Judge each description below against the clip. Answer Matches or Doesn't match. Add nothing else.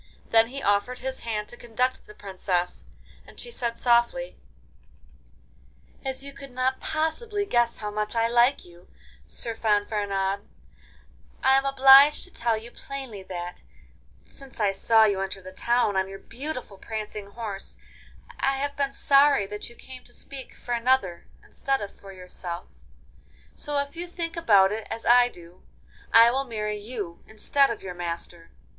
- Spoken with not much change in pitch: Doesn't match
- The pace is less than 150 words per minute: Doesn't match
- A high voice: Matches